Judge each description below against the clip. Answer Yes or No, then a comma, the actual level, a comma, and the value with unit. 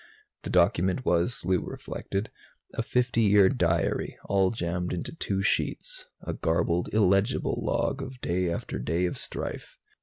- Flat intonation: No, average, 4.4 semitones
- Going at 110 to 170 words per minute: Yes, average, 145 wpm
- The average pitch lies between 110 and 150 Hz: No, very low, 95 Hz